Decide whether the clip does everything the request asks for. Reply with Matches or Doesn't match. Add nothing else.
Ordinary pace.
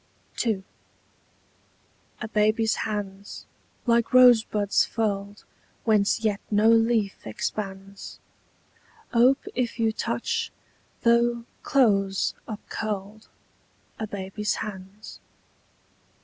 Doesn't match